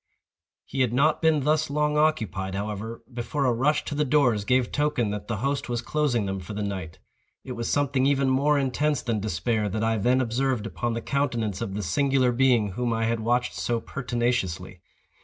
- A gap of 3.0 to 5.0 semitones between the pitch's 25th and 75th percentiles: Yes, average, 4.3 semitones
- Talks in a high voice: No, low, 120 Hz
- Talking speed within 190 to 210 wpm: Yes, average, 195 wpm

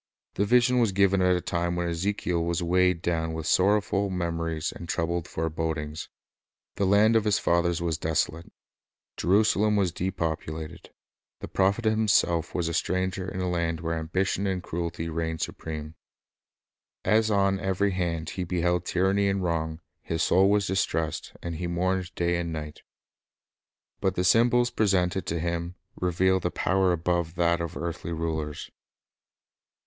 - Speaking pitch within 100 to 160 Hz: No, very low, 85 Hz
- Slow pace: No, average, 155 wpm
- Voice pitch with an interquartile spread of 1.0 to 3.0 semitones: Yes, narrow, 2.5 semitones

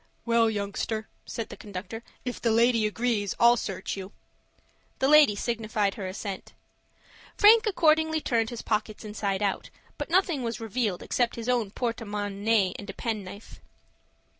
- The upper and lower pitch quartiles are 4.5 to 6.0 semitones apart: No, average, 3.0 semitones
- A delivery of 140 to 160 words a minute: Yes, average, 150 wpm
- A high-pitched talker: Yes, high, 225 Hz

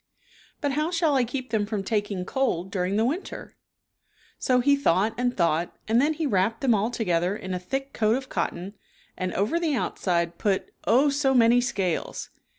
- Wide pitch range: Yes, wide, 6.0 semitones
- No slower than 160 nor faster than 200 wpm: Yes, average, 185 wpm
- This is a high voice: Yes, high, 225 Hz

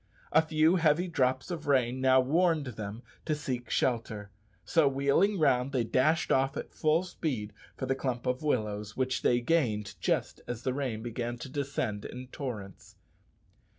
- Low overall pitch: Yes, low, 130 Hz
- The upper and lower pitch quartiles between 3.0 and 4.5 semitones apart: Yes, average, 4.1 semitones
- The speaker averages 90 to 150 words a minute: No, average, 165 wpm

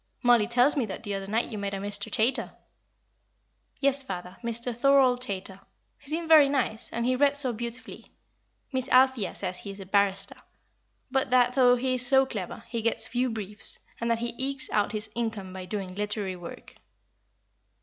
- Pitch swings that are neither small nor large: Yes, average, 4.1 semitones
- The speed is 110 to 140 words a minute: No, average, 185 wpm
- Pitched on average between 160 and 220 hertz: No, high, 235 Hz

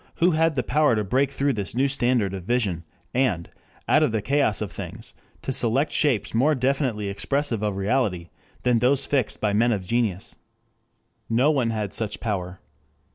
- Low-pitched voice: Yes, low, 115 Hz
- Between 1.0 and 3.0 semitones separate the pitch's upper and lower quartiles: No, average, 4.9 semitones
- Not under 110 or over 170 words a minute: No, average, 180 wpm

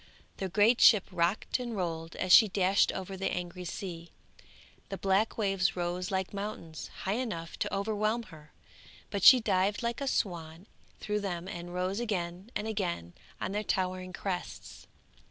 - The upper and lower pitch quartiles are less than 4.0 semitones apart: Yes, average, 3.0 semitones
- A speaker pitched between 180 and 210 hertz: Yes, high, 190 Hz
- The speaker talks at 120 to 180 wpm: Yes, average, 160 wpm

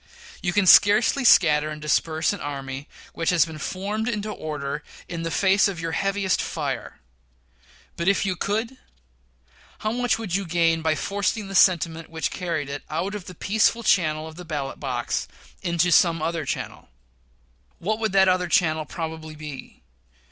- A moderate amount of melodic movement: Yes, average, 4.1 semitones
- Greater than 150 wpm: Yes, average, 170 wpm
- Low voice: No, medium, 170 Hz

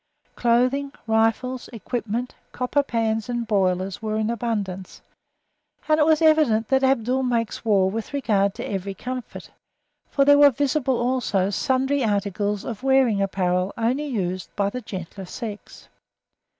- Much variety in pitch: No, average, 4.4 semitones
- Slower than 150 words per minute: Yes, average, 140 wpm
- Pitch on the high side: Yes, high, 230 Hz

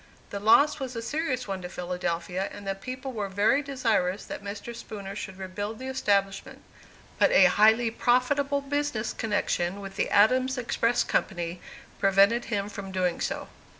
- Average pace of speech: Yes, average, 160 wpm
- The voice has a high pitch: Yes, high, 210 Hz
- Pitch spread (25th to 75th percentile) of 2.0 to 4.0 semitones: No, average, 4.6 semitones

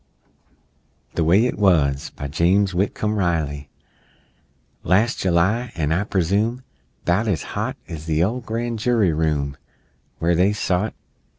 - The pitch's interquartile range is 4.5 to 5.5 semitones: Yes, average, 4.9 semitones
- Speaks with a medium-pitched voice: No, very low, 90 Hz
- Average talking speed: No, slow, 130 wpm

